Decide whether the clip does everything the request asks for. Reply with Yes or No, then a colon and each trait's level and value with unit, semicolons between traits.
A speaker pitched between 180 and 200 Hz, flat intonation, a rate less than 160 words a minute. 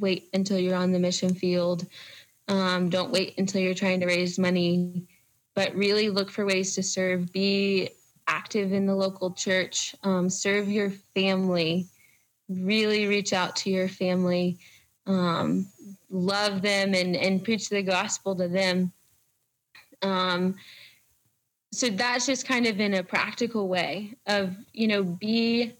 Yes: high, 190 Hz; narrow, 1.9 semitones; average, 145 wpm